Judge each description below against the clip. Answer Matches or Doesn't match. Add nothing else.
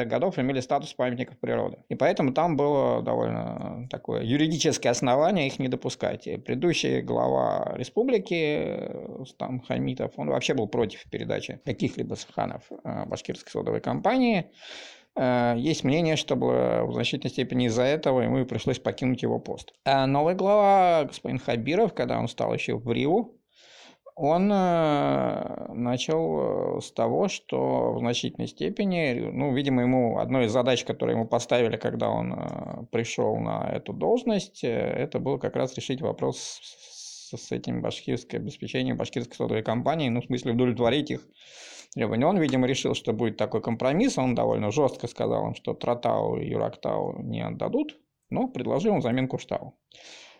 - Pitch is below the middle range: Matches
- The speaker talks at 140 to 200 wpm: Matches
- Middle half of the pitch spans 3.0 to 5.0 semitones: Matches